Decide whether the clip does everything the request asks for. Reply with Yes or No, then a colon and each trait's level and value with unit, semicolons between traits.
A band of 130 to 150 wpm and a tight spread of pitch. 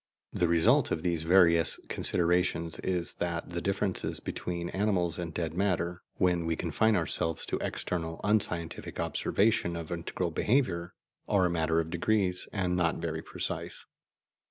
Yes: average, 145 wpm; narrow, 1.8 semitones